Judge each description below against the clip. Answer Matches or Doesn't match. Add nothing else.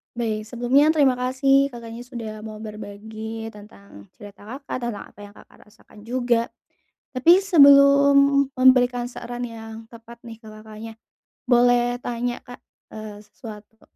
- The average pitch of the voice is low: Doesn't match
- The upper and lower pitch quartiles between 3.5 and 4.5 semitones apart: Doesn't match